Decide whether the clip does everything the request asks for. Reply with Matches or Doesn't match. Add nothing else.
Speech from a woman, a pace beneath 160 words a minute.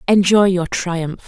Matches